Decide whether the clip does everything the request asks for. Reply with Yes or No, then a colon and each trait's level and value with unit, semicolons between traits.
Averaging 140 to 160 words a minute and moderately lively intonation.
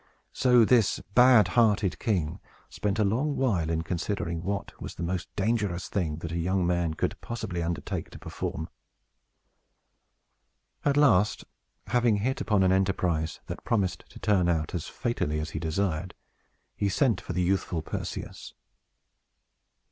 Yes: average, 150 wpm; average, 4.5 semitones